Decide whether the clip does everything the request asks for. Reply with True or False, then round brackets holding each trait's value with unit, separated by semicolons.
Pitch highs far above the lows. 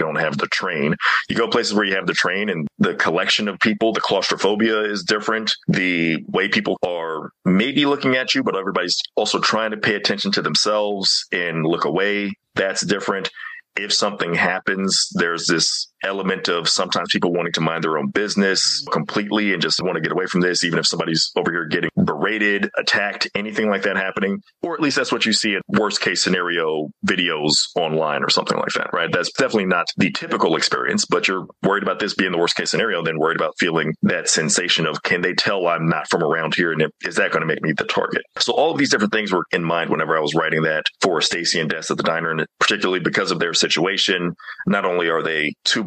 False (4.2 semitones)